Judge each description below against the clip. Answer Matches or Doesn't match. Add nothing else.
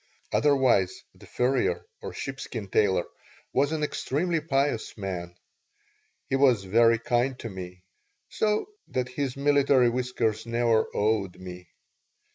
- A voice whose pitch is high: Doesn't match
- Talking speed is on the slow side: Matches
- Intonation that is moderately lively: Matches